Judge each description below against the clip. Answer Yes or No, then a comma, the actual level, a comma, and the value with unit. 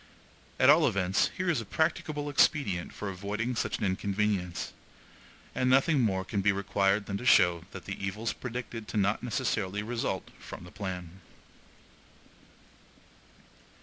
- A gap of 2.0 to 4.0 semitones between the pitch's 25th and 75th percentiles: No, average, 4.5 semitones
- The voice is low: Yes, low, 100 Hz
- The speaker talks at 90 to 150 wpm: Yes, average, 140 wpm